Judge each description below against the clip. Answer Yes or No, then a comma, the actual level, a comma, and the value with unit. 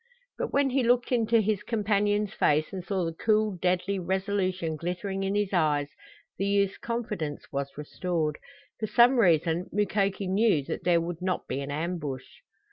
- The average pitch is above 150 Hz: Yes, high, 190 Hz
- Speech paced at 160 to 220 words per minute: Yes, average, 165 wpm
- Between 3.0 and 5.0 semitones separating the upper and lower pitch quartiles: Yes, average, 3.9 semitones